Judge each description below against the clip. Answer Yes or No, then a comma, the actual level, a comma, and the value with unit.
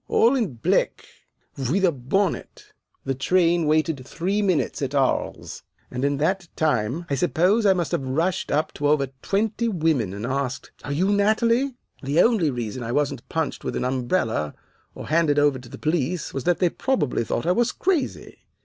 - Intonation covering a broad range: Yes, wide, 5.9 semitones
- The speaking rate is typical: Yes, average, 180 wpm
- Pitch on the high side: No, medium, 155 Hz